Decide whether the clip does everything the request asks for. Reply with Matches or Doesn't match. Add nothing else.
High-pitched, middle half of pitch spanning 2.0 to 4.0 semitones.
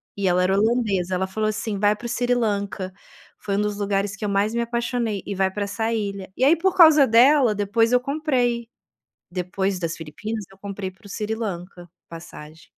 Matches